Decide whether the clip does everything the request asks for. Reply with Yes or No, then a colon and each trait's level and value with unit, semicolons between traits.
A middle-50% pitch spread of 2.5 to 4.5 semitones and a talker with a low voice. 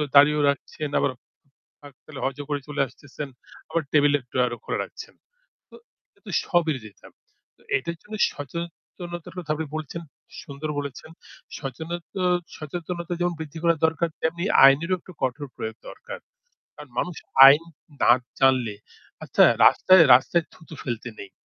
No: average, 3.6 semitones; medium, 150 Hz